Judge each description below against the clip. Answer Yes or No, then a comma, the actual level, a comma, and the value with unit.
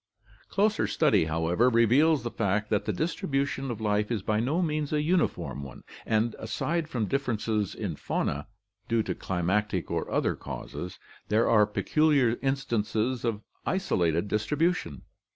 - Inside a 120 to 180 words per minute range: Yes, average, 145 wpm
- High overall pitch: No, low, 115 Hz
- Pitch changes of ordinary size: Yes, average, 5.0 semitones